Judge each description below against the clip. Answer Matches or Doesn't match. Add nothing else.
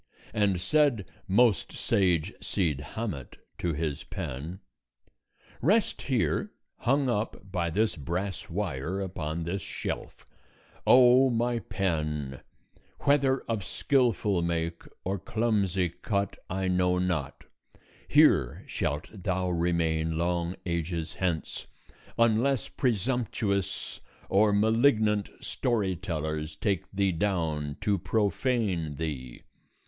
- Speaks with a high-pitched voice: Doesn't match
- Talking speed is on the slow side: Matches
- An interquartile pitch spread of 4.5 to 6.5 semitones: Matches